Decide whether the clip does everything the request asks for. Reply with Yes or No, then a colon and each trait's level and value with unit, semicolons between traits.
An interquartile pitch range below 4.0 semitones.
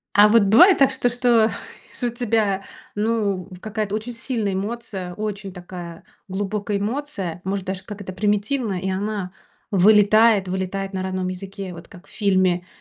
Yes: average, 2.7 semitones